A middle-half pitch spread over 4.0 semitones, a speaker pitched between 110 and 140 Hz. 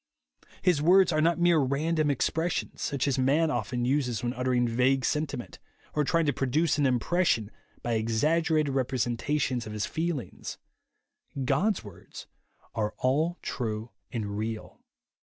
Yes: average, 4.8 semitones; low, 135 Hz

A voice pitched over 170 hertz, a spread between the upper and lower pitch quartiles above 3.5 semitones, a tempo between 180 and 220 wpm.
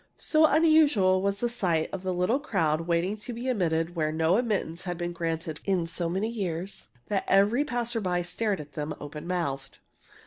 Yes: medium, 185 Hz; average, 5.0 semitones; average, 185 wpm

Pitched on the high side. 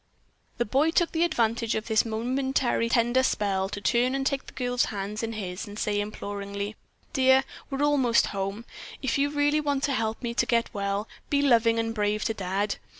Yes: high, 230 Hz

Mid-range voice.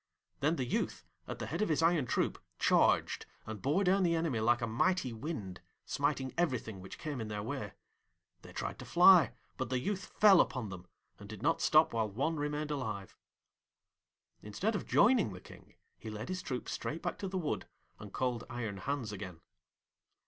No: low, 130 Hz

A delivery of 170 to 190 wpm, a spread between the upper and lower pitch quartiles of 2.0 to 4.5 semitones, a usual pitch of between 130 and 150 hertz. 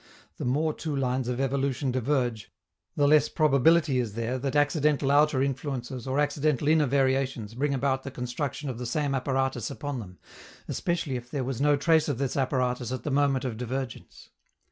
Yes: average, 180 wpm; narrow, 2.5 semitones; low, 135 Hz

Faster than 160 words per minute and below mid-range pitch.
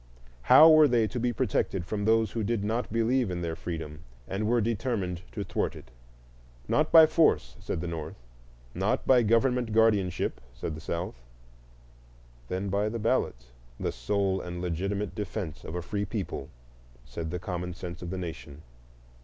Yes: average, 170 wpm; low, 100 Hz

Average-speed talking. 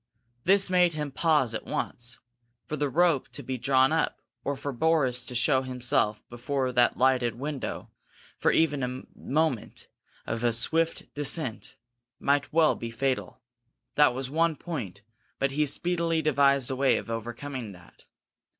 Yes: average, 155 wpm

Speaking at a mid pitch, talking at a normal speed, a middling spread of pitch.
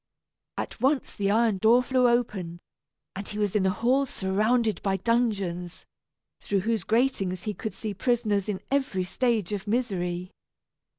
No: high, 210 Hz; average, 155 wpm; average, 3.9 semitones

